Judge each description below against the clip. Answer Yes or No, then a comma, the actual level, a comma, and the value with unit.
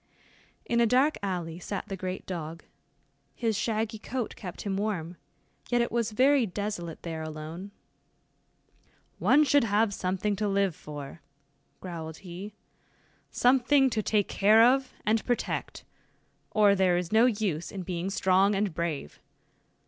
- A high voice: Yes, high, 200 Hz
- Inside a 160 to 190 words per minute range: No, average, 140 wpm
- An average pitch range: Yes, average, 4.3 semitones